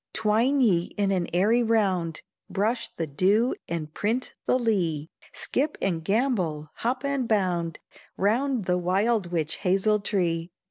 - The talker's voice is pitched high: Yes, high, 195 Hz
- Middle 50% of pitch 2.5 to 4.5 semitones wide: No, average, 5.0 semitones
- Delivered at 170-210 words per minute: No, average, 140 wpm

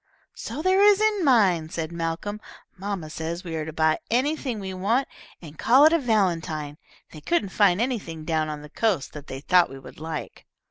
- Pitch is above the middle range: No, medium, 180 Hz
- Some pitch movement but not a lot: No, wide, 6.9 semitones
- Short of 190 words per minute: No, average, 195 wpm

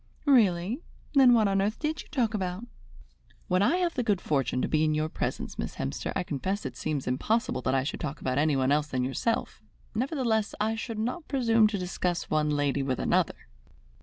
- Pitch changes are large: Yes, wide, 7.8 semitones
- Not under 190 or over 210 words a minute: Yes, average, 200 wpm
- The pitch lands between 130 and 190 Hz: Yes, medium, 185 Hz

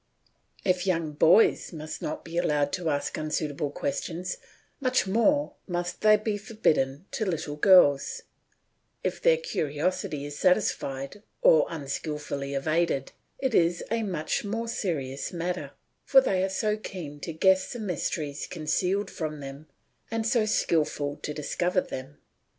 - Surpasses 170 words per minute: No, average, 140 wpm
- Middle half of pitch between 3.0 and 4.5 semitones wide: No, wide, 5.5 semitones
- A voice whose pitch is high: No, medium, 170 Hz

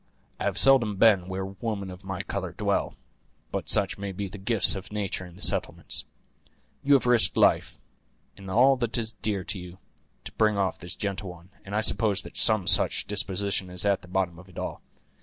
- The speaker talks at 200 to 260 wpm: Yes, fast, 205 wpm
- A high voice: No, low, 100 Hz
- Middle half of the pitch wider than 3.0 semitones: No, narrow, 2.5 semitones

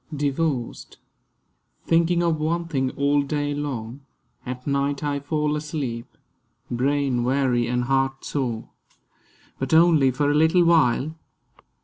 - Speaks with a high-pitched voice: No, medium, 140 Hz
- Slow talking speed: Yes, slow, 120 wpm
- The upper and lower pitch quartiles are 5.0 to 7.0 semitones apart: No, average, 2.8 semitones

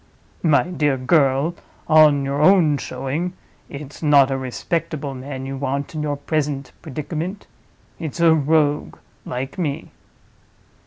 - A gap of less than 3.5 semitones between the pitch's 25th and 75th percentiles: Yes, narrow, 2.5 semitones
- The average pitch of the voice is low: No, medium, 145 Hz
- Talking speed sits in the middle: No, slow, 120 wpm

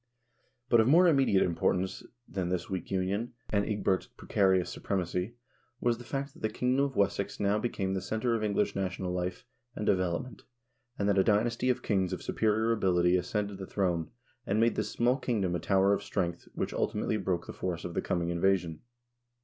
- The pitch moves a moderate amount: Yes, average, 3.5 semitones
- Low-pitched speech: Yes, low, 100 Hz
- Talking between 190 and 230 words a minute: Yes, average, 195 wpm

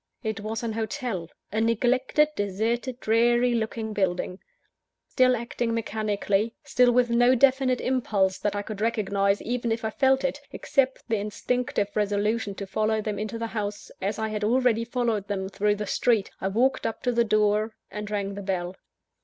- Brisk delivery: No, average, 175 wpm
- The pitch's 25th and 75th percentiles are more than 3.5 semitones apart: No, average, 2.8 semitones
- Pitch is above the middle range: Yes, high, 220 Hz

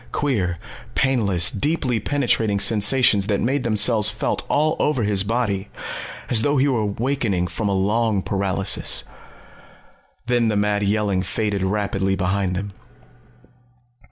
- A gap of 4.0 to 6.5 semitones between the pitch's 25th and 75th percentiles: No, average, 3.5 semitones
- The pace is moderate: No, slow, 130 wpm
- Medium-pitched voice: No, low, 105 Hz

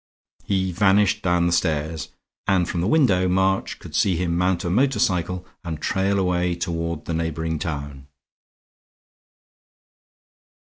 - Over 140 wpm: No, slow, 135 wpm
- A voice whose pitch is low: Yes, very low, 90 Hz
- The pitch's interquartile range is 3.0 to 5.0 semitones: No, narrow, 2.4 semitones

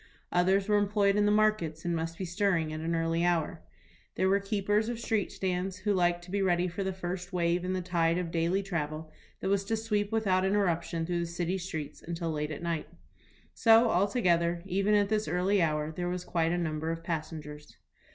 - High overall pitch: No, medium, 180 Hz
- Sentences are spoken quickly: Yes, fast, 210 wpm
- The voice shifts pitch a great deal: No, average, 3.1 semitones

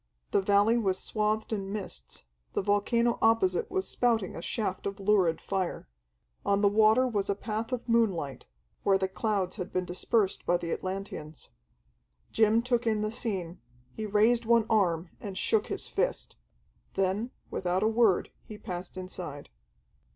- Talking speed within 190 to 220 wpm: No, average, 160 wpm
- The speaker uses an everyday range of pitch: Yes, average, 3.2 semitones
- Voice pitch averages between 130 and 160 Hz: No, high, 205 Hz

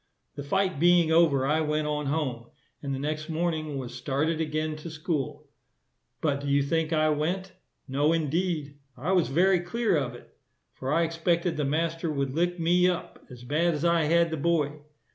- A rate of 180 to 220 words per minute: Yes, average, 185 wpm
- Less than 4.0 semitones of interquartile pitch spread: Yes, average, 2.9 semitones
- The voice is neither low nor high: Yes, medium, 155 Hz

